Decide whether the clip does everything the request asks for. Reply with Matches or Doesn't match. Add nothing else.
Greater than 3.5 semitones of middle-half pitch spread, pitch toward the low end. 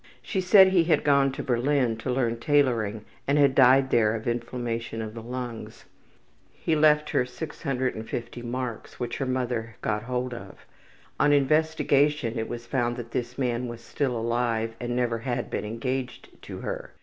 Doesn't match